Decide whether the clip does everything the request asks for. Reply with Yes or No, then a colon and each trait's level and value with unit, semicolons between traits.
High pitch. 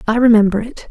Yes: high, 225 Hz